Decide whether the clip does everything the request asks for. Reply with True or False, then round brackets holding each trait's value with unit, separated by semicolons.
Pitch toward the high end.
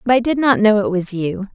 True (215 Hz)